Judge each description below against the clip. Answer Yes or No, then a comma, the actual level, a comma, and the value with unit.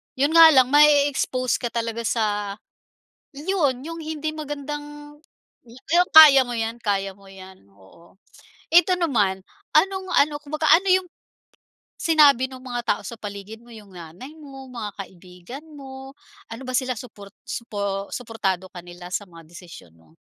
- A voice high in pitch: Yes, very high, 250 Hz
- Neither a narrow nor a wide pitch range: No, wide, 6.8 semitones